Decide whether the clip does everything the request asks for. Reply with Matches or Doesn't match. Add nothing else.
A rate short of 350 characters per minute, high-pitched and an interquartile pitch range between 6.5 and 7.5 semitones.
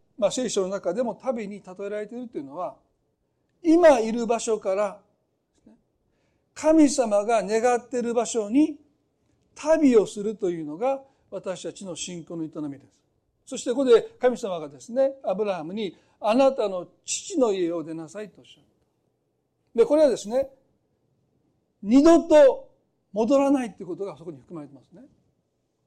Matches